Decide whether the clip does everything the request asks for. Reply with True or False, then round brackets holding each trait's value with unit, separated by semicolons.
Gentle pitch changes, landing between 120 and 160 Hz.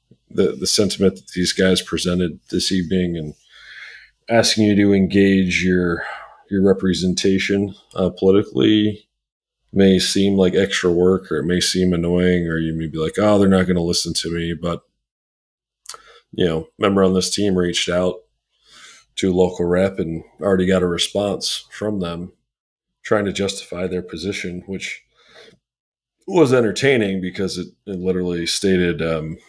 False (2.0 semitones; 95 Hz)